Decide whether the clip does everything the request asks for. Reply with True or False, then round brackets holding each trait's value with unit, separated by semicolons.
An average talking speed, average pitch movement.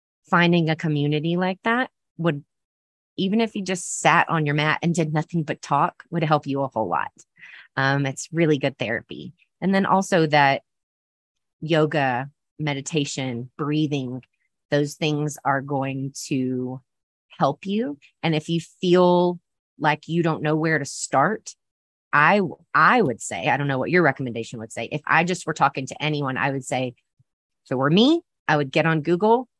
True (175 wpm; 3.9 semitones)